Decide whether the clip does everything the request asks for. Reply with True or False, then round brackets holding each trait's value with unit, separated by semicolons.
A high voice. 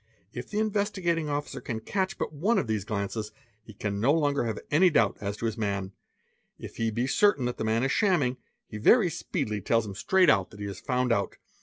False (120 Hz)